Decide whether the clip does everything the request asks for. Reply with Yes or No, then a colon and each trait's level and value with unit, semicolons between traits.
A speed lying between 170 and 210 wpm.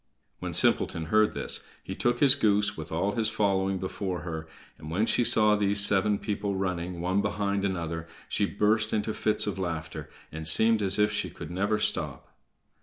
Yes: average, 180 wpm